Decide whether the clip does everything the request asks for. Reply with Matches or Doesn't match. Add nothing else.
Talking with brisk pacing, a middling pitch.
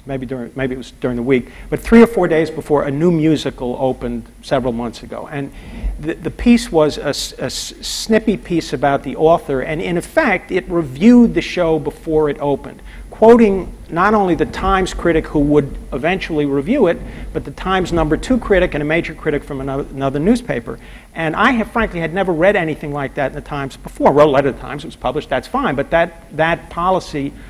Matches